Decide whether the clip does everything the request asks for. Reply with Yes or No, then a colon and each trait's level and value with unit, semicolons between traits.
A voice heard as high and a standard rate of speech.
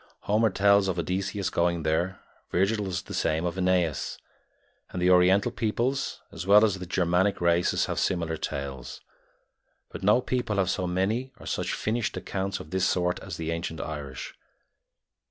No: very low, 95 Hz; average, 165 wpm